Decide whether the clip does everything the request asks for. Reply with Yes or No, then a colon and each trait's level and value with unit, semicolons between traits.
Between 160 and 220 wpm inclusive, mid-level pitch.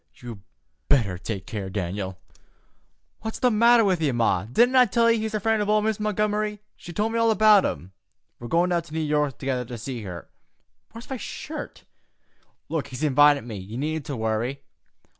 Yes: average, 185 wpm; medium, 150 Hz